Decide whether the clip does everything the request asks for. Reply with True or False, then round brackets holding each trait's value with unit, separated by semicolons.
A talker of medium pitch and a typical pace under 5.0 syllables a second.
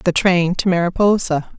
True (180 Hz; 4.6 syllables/s)